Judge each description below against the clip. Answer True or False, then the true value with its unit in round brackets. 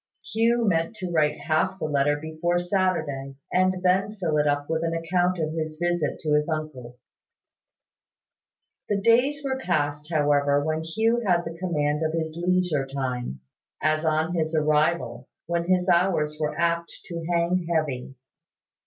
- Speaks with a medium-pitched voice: True (165 Hz)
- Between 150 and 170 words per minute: True (155 wpm)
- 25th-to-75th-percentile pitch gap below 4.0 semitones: True (3.1 semitones)